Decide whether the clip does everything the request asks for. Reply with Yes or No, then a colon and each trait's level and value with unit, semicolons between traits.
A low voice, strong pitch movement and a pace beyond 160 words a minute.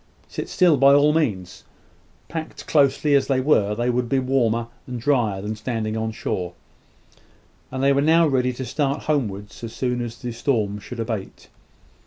No: low, 125 Hz; average, 3.9 semitones; average, 175 wpm